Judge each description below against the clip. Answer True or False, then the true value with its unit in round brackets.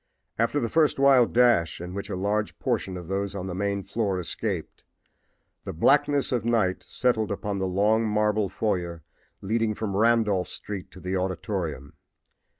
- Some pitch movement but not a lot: True (3.5 semitones)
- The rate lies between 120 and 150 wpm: False (160 wpm)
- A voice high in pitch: False (100 Hz)